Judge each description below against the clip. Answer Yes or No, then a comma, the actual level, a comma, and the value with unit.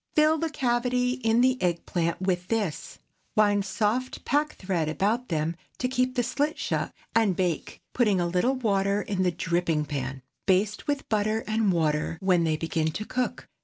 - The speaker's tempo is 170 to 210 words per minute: Yes, average, 175 wpm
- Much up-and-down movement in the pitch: Yes, wide, 6.3 semitones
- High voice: Yes, high, 205 Hz